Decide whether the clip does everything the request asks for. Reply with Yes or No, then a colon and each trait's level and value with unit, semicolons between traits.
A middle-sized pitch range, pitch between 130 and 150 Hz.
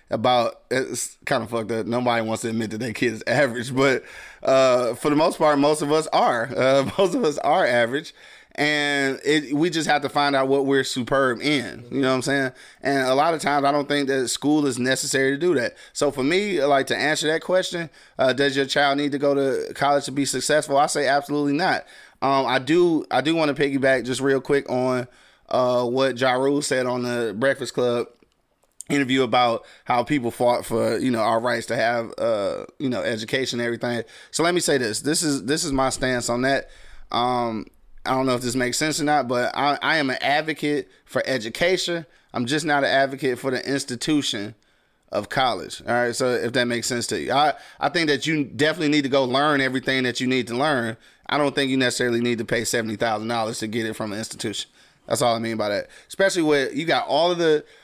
Yes: average, 3.0 semitones; low, 135 Hz